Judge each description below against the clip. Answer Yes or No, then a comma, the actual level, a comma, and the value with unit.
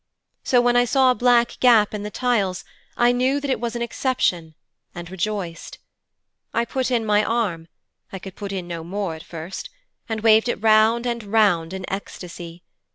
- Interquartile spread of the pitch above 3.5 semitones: Yes, average, 4.8 semitones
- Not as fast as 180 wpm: No, average, 185 wpm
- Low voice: No, high, 215 Hz